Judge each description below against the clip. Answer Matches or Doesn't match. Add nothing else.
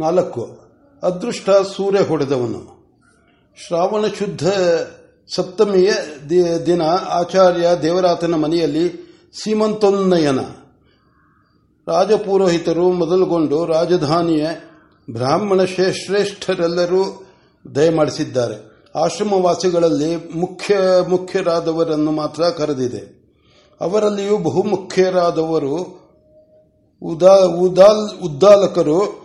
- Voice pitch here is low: Doesn't match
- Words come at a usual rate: Doesn't match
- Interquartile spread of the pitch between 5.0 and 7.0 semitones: Doesn't match